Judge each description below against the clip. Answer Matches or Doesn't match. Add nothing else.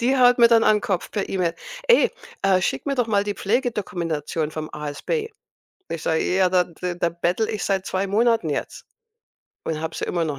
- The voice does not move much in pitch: Doesn't match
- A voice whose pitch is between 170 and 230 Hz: Matches